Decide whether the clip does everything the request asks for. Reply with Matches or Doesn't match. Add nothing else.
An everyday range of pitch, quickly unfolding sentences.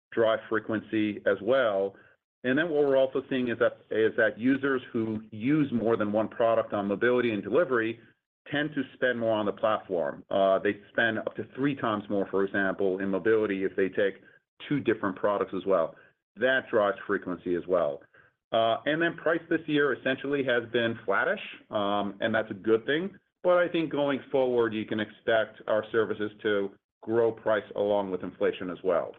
Doesn't match